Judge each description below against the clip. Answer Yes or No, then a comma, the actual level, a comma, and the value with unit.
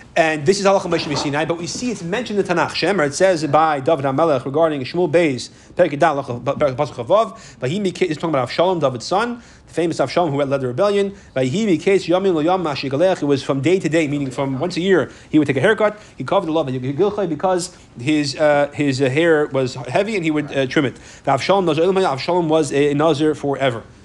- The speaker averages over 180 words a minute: Yes, average, 200 wpm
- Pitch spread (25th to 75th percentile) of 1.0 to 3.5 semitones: No, average, 4.5 semitones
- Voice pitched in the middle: Yes, medium, 155 Hz